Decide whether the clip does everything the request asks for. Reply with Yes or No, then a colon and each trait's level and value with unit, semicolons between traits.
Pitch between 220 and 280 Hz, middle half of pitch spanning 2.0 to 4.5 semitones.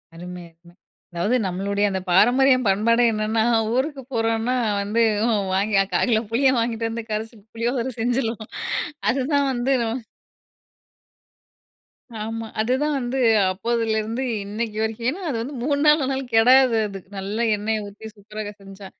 Yes: high, 225 Hz; average, 3.3 semitones